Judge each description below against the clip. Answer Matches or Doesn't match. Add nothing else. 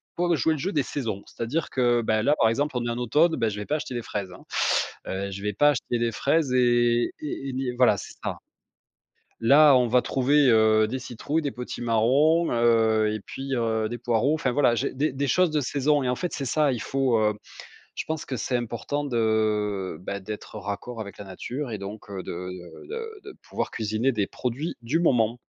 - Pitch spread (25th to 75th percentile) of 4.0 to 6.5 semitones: Matches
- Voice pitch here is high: Doesn't match